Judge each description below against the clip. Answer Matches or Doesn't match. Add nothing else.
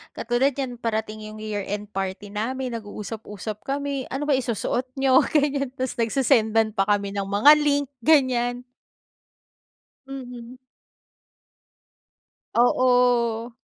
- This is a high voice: Matches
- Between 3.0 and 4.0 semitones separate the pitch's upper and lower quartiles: Matches